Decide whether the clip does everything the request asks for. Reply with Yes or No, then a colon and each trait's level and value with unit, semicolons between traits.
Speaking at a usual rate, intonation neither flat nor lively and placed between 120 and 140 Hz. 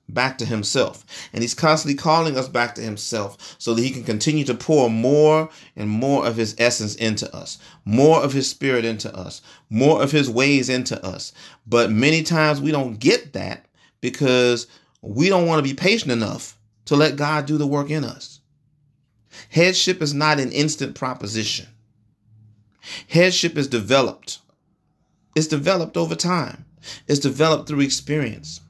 Yes: average, 165 wpm; average, 5.0 semitones; low, 135 Hz